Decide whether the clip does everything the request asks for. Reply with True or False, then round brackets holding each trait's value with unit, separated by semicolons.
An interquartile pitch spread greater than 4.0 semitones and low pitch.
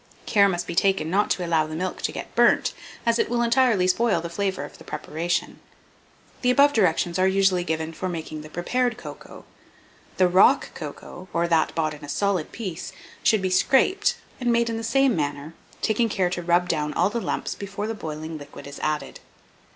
False (5.4 semitones; 185 Hz)